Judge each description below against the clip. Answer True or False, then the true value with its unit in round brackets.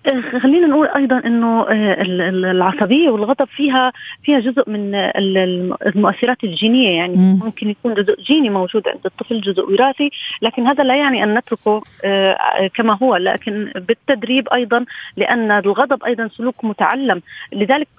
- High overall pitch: True (230 Hz)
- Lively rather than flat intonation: False (4.4 semitones)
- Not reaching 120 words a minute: False (130 wpm)